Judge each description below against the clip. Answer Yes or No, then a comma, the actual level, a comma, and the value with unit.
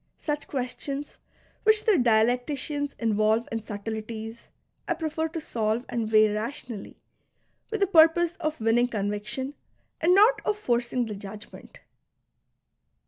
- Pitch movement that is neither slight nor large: No, wide, 6.2 semitones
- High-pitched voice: Yes, high, 245 Hz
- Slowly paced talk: Yes, slow, 125 wpm